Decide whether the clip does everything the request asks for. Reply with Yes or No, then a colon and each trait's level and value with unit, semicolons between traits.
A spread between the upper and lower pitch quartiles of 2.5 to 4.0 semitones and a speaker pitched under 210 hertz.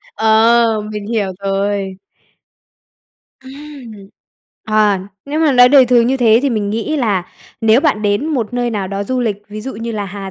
No: average, 3.5 semitones; high, 225 Hz